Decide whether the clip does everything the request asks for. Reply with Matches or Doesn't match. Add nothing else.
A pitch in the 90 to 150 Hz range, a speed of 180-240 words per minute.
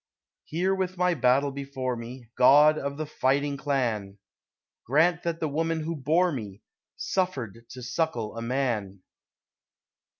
Doesn't match